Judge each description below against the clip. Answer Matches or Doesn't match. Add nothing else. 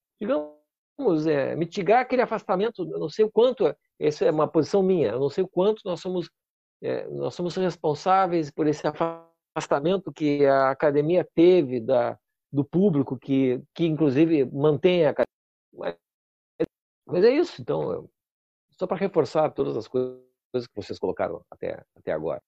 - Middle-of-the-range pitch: Matches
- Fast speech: Doesn't match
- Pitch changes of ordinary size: Matches